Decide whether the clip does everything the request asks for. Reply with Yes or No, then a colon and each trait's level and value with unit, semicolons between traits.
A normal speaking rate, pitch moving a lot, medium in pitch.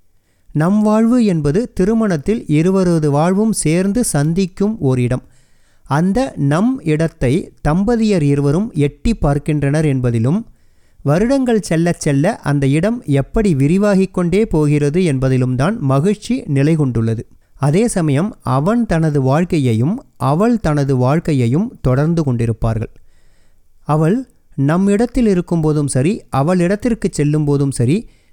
Yes: average, 105 wpm; wide, 6.4 semitones; medium, 155 Hz